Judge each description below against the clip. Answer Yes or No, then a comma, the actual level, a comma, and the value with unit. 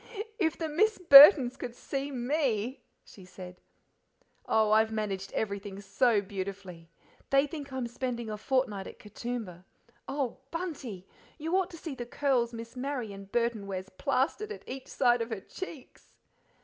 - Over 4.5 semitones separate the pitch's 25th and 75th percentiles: Yes, average, 5.3 semitones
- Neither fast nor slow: Yes, average, 150 wpm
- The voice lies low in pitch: No, high, 240 Hz